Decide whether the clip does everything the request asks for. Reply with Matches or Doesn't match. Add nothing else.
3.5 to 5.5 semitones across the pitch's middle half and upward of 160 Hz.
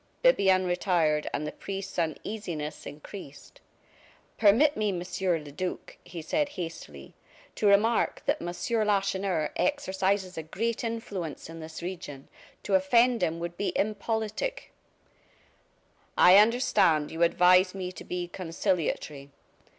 Matches